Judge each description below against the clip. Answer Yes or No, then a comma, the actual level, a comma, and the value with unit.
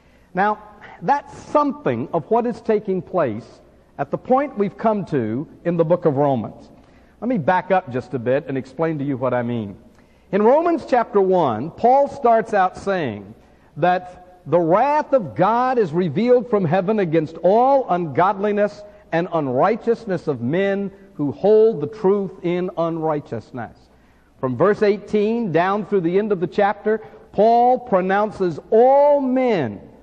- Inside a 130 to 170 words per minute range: Yes, average, 155 wpm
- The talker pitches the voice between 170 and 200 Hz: Yes, high, 190 Hz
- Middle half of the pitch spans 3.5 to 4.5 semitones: No, average, 5.1 semitones